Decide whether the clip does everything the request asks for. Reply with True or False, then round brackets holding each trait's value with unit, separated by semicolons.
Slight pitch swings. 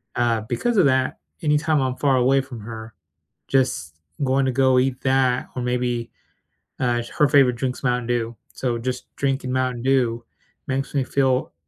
True (1.8 semitones)